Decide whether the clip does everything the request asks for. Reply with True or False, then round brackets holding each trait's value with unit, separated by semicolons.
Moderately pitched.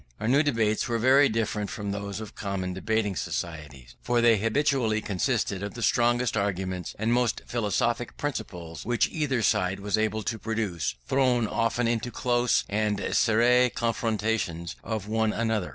False (110 Hz)